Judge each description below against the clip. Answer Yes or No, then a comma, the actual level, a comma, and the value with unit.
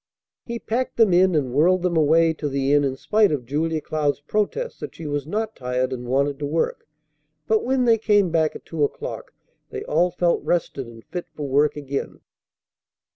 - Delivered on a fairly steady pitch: No, average, 4.6 semitones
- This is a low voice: No, medium, 155 Hz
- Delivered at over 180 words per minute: Yes, average, 195 wpm